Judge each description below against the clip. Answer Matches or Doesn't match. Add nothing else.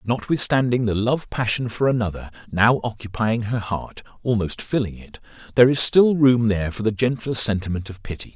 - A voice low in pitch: Matches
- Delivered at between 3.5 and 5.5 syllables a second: Matches